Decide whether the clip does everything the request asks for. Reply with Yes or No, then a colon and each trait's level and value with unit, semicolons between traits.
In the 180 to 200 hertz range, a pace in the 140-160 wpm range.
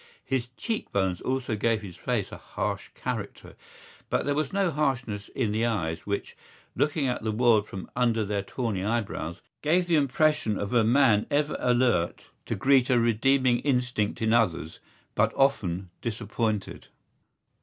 No: low, 120 Hz; average, 155 wpm